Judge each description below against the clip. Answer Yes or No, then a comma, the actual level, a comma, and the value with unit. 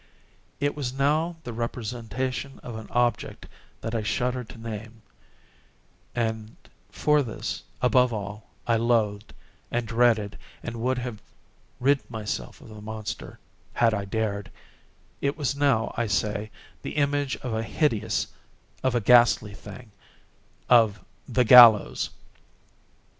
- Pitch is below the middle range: Yes, low, 115 Hz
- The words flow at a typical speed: No, slow, 120 wpm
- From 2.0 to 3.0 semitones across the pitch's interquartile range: Yes, average, 2.7 semitones